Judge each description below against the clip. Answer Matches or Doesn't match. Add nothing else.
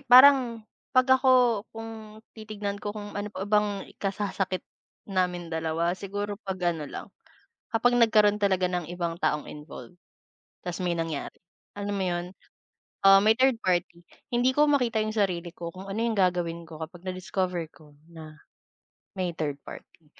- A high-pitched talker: Matches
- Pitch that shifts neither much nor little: Matches